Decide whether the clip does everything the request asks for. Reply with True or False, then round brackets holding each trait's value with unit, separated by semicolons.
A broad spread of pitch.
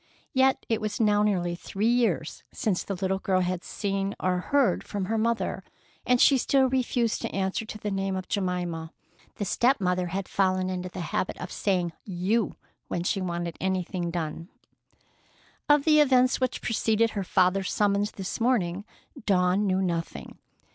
False (3.6 semitones)